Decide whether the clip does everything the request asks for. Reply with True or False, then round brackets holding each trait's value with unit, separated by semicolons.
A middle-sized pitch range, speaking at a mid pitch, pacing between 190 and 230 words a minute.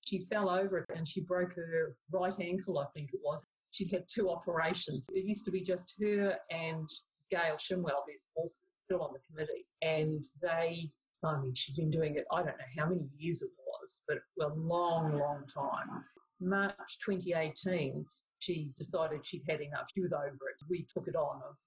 True (3.4 semitones; 170 Hz; 195 wpm)